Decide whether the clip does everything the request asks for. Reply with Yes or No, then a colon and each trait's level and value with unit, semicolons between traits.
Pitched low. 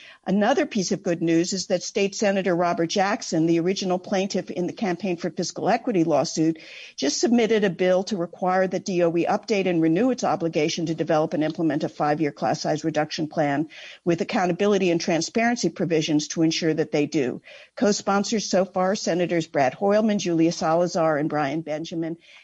No: medium, 175 Hz